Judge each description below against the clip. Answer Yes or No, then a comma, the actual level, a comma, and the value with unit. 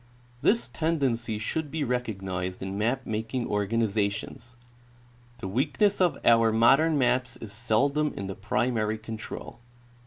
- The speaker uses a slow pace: Yes, slow, 125 wpm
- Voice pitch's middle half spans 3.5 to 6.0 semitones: Yes, average, 3.8 semitones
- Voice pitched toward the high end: No, low, 115 Hz